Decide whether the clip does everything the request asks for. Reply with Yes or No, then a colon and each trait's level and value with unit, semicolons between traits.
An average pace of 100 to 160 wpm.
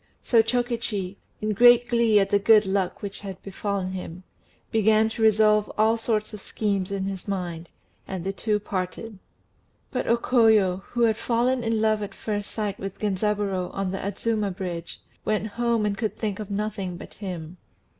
No: average, 175 wpm